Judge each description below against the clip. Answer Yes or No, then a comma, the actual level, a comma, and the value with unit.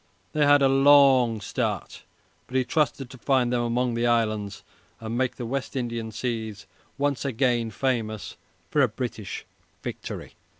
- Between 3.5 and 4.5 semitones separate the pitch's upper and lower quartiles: No, average, 3.1 semitones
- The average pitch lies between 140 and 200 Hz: No, low, 120 Hz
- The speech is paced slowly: No, average, 160 wpm